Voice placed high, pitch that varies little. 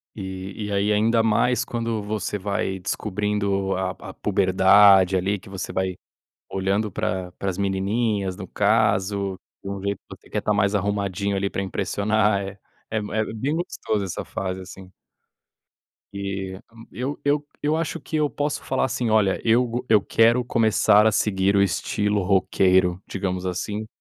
No: low, 100 Hz; narrow, 2.3 semitones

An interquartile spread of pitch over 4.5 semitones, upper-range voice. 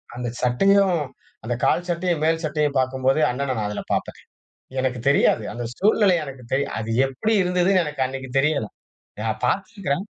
No: wide, 5.6 semitones; medium, 140 Hz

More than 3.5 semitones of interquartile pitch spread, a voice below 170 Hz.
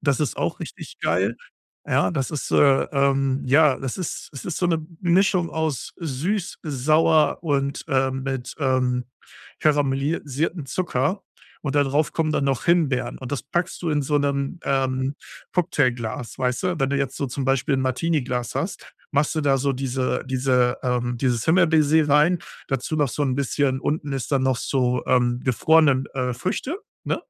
No: average, 3.2 semitones; medium, 140 Hz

